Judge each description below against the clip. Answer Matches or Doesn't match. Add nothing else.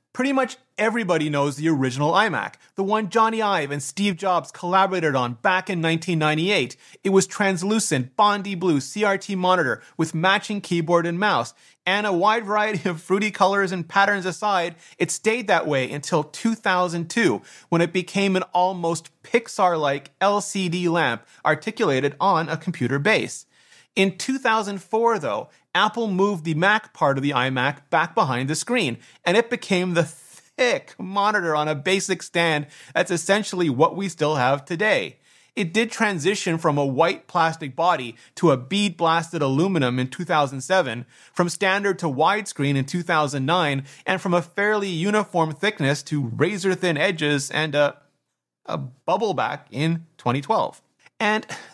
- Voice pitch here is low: Doesn't match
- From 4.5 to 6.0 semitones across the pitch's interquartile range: Matches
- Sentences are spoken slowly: Doesn't match